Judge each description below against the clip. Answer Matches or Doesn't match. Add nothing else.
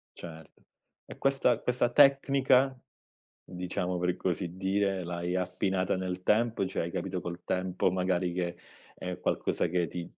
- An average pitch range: Doesn't match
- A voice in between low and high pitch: Doesn't match